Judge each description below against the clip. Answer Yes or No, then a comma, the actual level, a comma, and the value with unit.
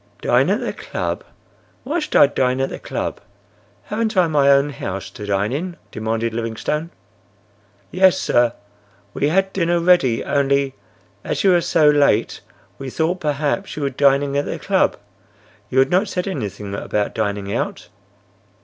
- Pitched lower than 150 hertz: Yes, medium, 140 Hz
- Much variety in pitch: Yes, wide, 7.2 semitones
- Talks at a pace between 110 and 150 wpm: No, average, 160 wpm